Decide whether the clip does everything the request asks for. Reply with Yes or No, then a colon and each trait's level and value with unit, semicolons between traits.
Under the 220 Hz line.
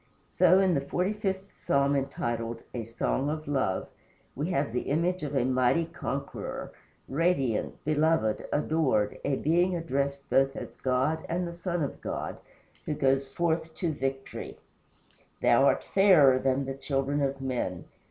Yes: medium, 140 Hz